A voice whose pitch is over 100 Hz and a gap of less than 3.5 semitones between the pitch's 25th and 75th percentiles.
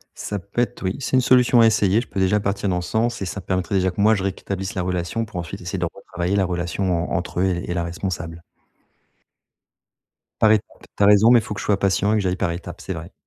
No: very low, 95 Hz; average, 2.8 semitones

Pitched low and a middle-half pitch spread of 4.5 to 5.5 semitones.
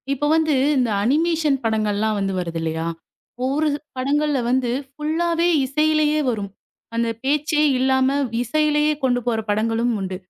No: very high, 265 Hz; average, 5.2 semitones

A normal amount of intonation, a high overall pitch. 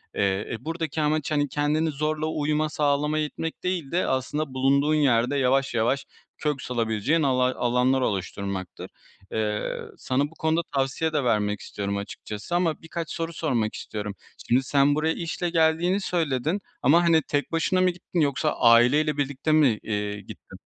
No: average, 4.5 semitones; medium, 145 Hz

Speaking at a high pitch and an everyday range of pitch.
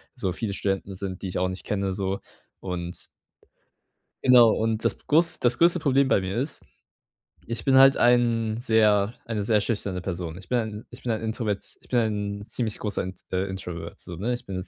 No: low, 105 Hz; average, 3.9 semitones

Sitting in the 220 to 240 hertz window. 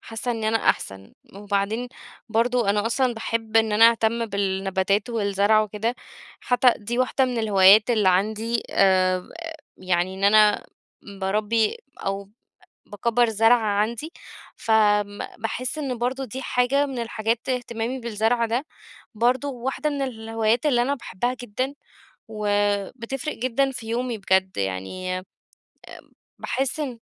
Yes: high, 225 Hz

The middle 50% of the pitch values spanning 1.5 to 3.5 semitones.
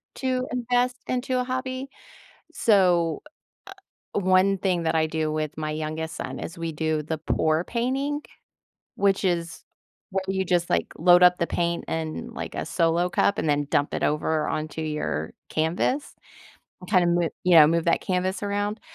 No: average, 4.1 semitones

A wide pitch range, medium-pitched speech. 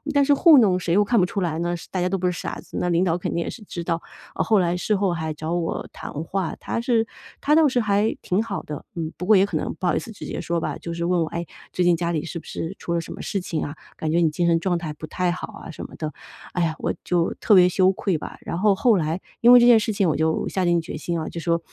No: average, 3.1 semitones; medium, 175 Hz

